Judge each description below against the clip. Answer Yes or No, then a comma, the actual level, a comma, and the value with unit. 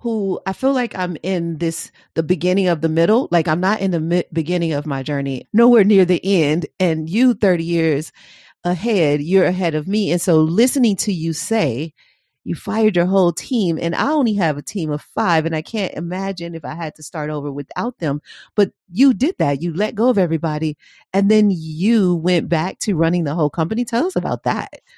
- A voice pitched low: No, medium, 175 Hz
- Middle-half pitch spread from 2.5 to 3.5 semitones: No, average, 4.4 semitones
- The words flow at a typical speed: No, fast, 215 wpm